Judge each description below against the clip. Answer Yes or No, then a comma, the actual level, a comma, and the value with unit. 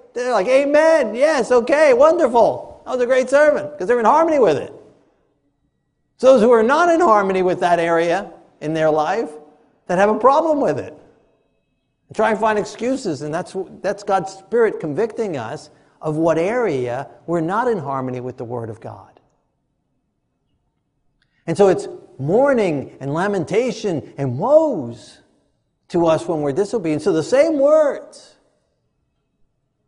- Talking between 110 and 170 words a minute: Yes, average, 155 wpm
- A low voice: No, high, 190 Hz